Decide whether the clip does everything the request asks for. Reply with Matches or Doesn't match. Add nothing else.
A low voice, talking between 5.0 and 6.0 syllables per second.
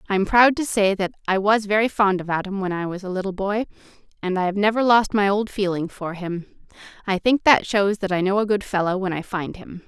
Doesn't match